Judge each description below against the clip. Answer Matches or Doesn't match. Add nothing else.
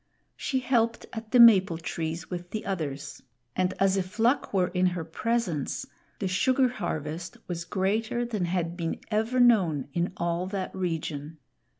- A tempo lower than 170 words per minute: Matches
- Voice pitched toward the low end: Doesn't match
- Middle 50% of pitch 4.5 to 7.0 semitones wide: Matches